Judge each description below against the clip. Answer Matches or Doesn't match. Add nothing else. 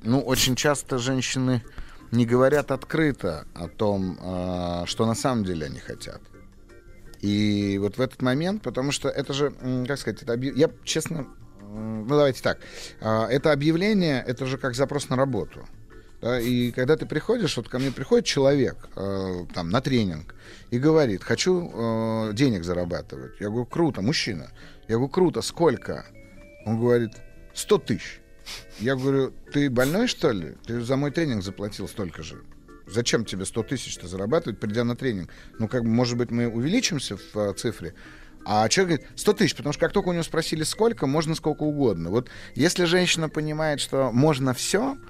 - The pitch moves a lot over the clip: Matches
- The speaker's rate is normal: Doesn't match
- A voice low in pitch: Matches